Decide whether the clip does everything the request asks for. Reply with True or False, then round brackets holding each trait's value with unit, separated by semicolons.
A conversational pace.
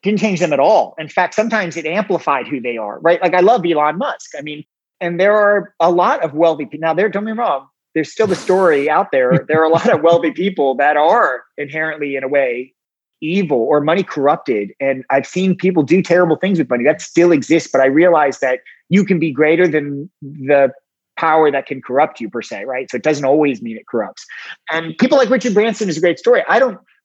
False (235 wpm)